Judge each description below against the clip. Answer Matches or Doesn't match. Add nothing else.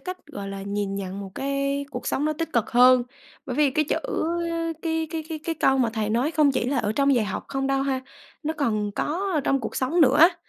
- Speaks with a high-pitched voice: Matches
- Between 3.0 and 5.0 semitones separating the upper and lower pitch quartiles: Doesn't match